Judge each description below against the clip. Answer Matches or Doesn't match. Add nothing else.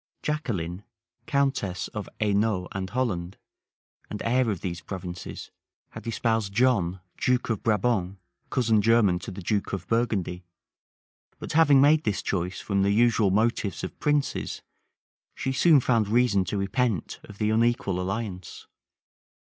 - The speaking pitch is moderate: Doesn't match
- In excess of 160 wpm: Doesn't match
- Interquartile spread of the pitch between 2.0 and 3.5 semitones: Doesn't match